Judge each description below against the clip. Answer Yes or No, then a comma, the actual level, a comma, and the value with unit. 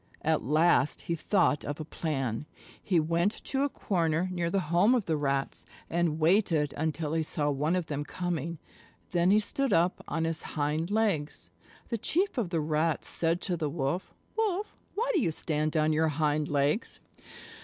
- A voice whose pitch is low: No, medium, 165 Hz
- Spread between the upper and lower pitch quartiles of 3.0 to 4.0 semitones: Yes, average, 3.4 semitones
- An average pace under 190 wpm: Yes, average, 180 wpm